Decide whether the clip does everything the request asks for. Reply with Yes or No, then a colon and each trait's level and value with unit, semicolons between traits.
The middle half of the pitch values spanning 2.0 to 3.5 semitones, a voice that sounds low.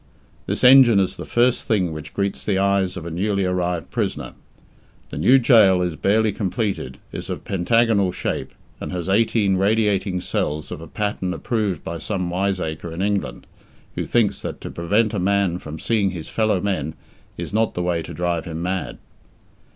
Yes: average, 3.2 semitones; very low, 95 Hz